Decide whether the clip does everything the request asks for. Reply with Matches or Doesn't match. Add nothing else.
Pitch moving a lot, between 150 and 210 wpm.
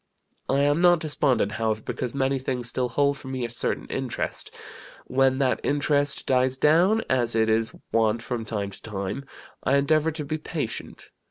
Doesn't match